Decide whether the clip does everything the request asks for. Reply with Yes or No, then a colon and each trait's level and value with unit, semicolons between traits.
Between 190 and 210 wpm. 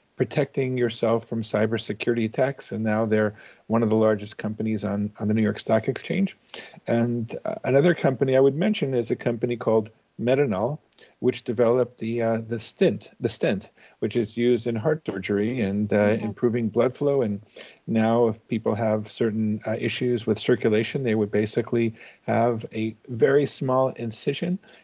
No: average, 165 wpm